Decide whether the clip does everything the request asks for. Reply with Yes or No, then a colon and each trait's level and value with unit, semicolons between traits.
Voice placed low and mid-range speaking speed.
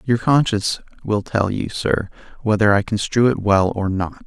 Yes: low, 105 Hz; average, 185 wpm